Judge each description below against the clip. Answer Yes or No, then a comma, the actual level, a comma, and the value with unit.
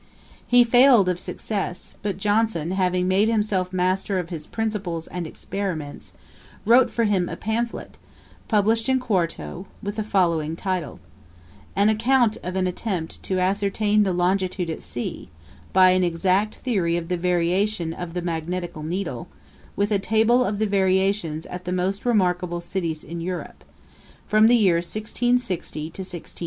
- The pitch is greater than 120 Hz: Yes, high, 190 Hz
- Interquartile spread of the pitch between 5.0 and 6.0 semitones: No, average, 3.4 semitones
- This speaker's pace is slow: No, average, 155 wpm